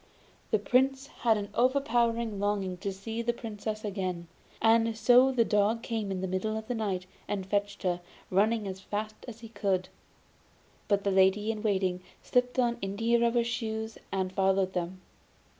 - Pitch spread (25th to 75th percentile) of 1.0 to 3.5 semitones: Yes, average, 3.2 semitones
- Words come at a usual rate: Yes, average, 170 wpm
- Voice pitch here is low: No, high, 215 Hz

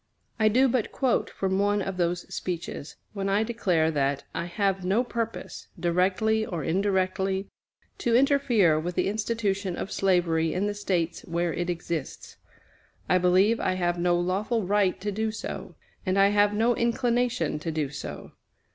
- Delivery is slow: No, average, 165 wpm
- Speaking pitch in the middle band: No, high, 195 Hz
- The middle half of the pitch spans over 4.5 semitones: No, average, 3.7 semitones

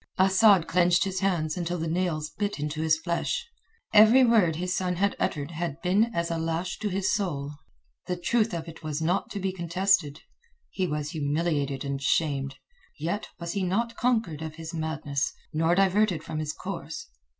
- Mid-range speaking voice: Yes, medium, 170 Hz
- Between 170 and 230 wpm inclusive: Yes, average, 180 wpm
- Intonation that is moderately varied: Yes, average, 3.6 semitones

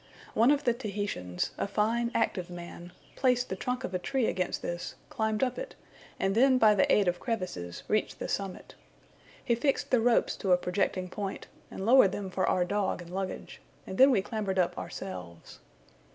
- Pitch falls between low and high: No, high, 200 Hz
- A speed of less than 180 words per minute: No, average, 190 wpm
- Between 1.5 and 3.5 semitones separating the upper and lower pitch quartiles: No, average, 4.4 semitones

